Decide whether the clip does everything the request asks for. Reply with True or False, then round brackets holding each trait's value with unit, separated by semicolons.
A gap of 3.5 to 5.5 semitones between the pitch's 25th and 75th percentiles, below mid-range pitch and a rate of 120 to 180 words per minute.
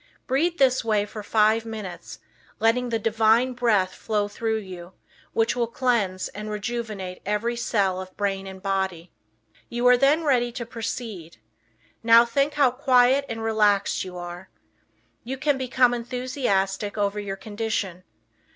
False (3.8 semitones; 225 Hz; 145 wpm)